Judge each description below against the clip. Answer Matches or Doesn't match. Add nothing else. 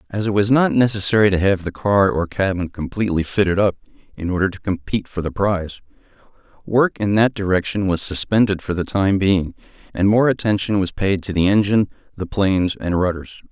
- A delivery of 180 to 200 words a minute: Matches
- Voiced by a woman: Doesn't match